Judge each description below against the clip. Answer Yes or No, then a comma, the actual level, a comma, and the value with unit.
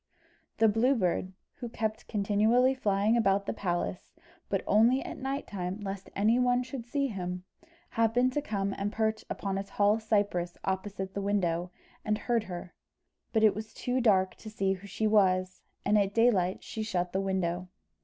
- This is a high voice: Yes, high, 205 Hz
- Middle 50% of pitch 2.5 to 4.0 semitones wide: Yes, average, 2.9 semitones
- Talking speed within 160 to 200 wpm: Yes, average, 175 wpm